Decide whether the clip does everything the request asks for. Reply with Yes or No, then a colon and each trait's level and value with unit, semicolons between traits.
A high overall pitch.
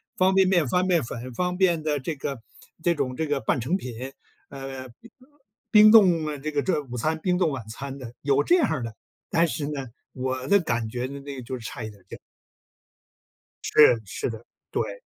No: medium, 140 Hz